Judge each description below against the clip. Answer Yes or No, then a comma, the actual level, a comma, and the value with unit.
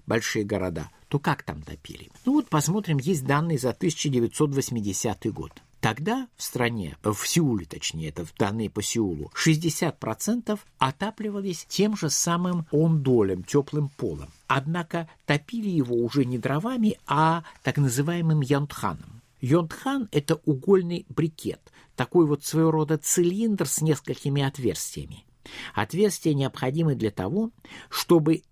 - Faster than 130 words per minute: No, average, 125 wpm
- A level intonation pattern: No, average, 5.1 semitones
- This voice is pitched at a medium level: Yes, medium, 155 Hz